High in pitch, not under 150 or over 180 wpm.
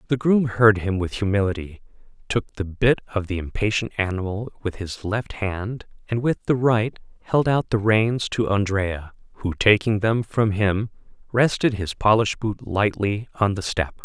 No: low, 105 Hz; average, 170 wpm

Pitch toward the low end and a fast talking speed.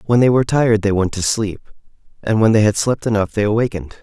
Yes: low, 110 Hz; fast, 240 wpm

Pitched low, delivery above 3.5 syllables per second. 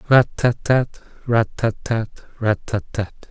No: low, 115 Hz; 3.4 syllables/s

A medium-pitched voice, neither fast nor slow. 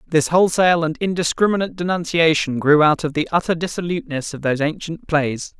Yes: medium, 160 Hz; average, 160 wpm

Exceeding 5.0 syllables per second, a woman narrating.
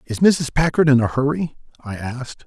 No: 5.2 syllables/s; male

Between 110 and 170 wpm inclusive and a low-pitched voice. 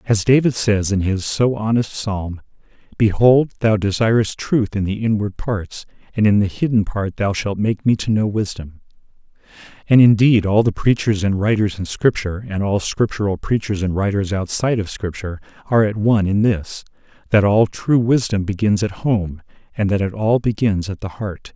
No: average, 185 wpm; low, 105 Hz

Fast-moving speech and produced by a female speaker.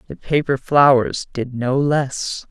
No: average, 145 wpm; female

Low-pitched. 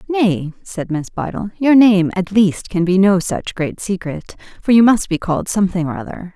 No: high, 190 Hz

